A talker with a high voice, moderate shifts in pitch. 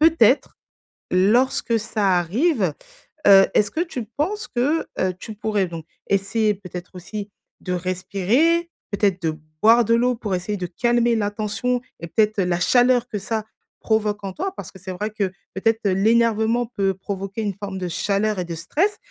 Yes: high, 210 Hz; average, 3.8 semitones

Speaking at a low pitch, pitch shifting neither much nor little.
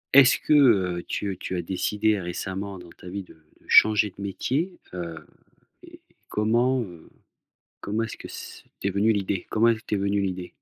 Yes: low, 100 Hz; average, 3.2 semitones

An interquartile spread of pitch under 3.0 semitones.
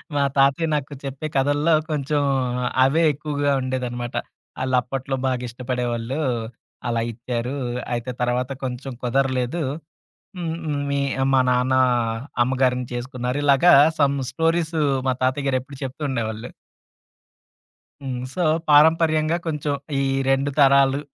Yes: narrow, 2.5 semitones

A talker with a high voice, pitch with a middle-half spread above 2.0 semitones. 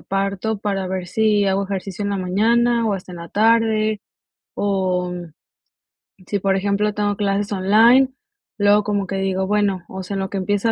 No: high, 200 Hz; narrow, 1.7 semitones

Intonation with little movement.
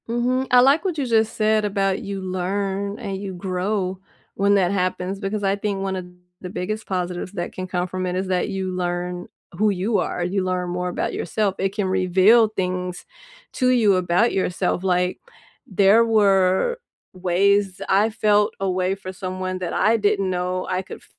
Yes: narrow, 2.1 semitones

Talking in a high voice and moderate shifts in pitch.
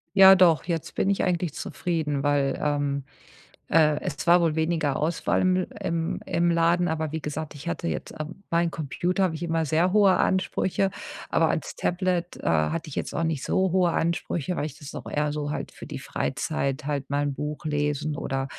No: medium, 160 Hz; average, 3.1 semitones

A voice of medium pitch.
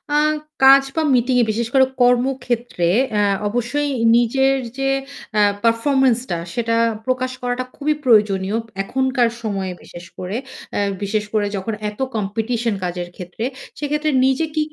No: high, 240 Hz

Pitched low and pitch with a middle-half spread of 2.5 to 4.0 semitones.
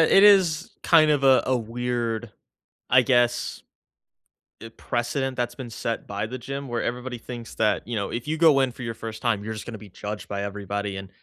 Yes: low, 120 Hz; average, 3.1 semitones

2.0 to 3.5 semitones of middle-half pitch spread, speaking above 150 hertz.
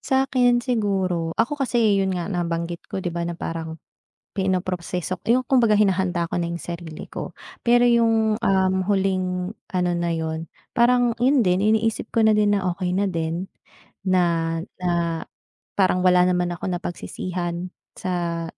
No: average, 4.0 semitones; medium, 185 Hz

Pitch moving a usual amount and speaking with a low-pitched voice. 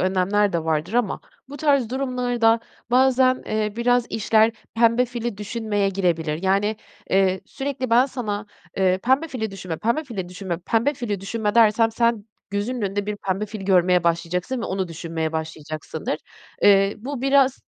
No: average, 4.5 semitones; high, 210 Hz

